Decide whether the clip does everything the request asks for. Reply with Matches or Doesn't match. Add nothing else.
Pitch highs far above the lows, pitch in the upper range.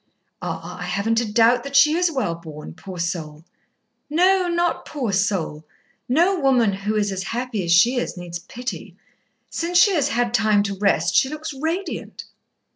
Matches